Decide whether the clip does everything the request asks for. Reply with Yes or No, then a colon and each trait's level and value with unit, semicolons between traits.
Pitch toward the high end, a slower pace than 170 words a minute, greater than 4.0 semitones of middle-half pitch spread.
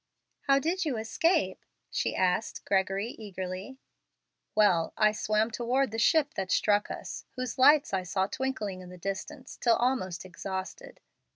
Yes: high, 215 Hz; average, 150 wpm; wide, 5.6 semitones